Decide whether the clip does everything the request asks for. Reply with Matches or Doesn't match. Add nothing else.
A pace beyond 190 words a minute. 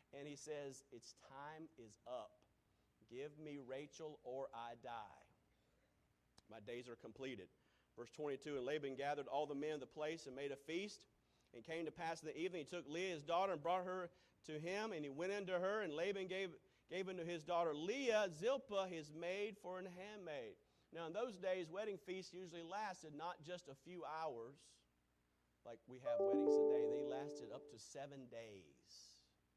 Doesn't match